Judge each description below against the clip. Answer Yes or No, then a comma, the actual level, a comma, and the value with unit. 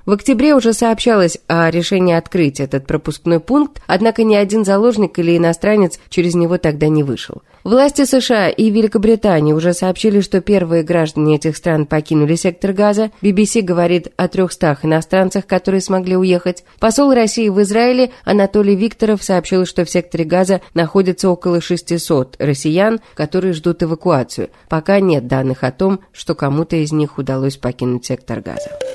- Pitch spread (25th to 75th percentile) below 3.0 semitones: No, average, 4.3 semitones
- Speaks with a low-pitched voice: No, medium, 180 Hz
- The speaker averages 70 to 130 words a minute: No, average, 155 wpm